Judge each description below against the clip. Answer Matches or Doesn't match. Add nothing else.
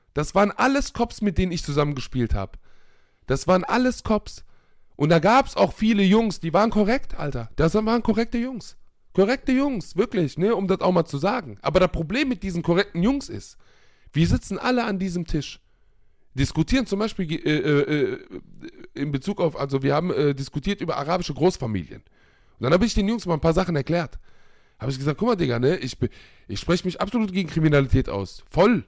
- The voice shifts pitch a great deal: Matches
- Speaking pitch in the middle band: Matches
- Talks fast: Matches